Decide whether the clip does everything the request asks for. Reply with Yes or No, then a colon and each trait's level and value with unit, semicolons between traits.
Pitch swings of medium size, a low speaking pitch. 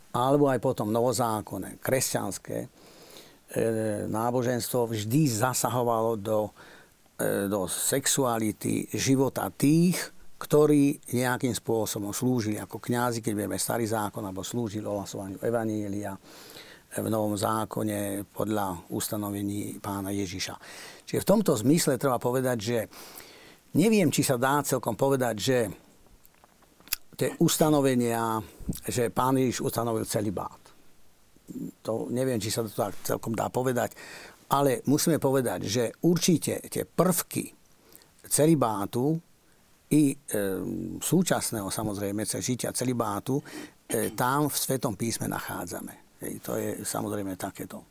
Yes: average, 4.2 semitones; low, 120 Hz